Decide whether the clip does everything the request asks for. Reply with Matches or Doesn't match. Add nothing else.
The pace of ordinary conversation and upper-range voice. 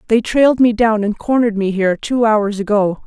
Doesn't match